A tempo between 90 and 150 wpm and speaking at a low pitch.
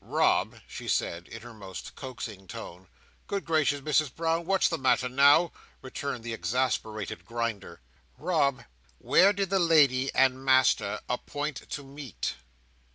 Yes: average, 140 wpm; low, 130 Hz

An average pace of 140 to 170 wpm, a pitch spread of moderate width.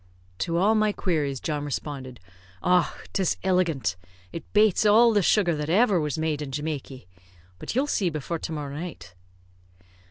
Yes: average, 160 wpm; average, 5.0 semitones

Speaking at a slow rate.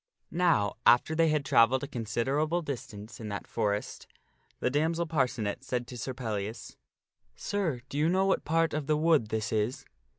No: average, 175 wpm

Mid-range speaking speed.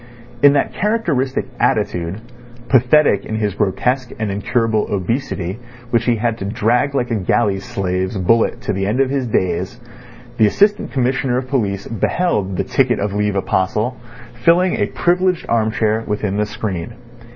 Yes: average, 160 wpm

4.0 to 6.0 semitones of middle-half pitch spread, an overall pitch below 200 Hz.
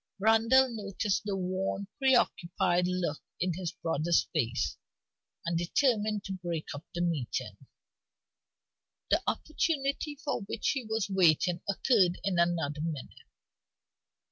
Yes: average, 4.5 semitones; medium, 185 Hz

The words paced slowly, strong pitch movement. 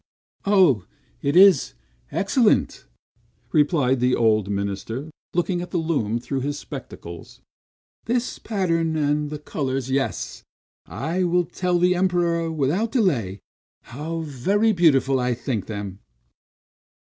Yes: slow, 120 wpm; wide, 6.1 semitones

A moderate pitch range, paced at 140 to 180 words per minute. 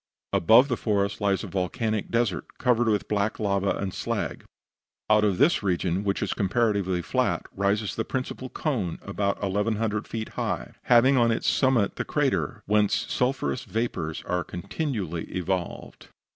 Yes: average, 3.2 semitones; average, 155 wpm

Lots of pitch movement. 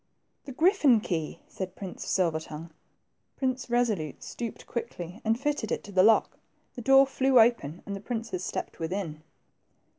Yes: wide, 5.8 semitones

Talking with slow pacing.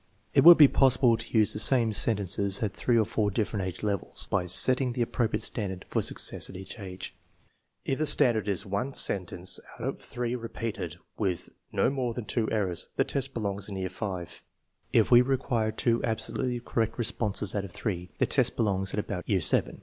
No: fast, 205 wpm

